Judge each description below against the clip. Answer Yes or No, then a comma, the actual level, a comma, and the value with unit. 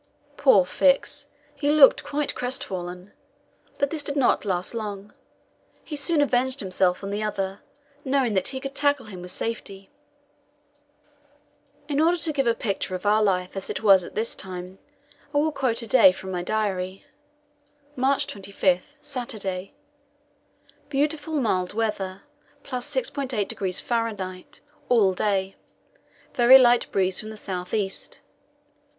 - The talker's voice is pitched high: Yes, high, 215 Hz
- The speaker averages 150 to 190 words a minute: No, average, 140 wpm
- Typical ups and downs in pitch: No, wide, 6.1 semitones